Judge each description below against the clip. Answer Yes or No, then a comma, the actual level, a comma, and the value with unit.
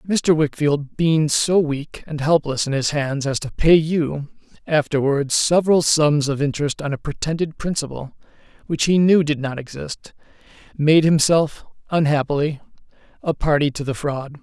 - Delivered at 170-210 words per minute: No, average, 155 wpm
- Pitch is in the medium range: Yes, medium, 150 Hz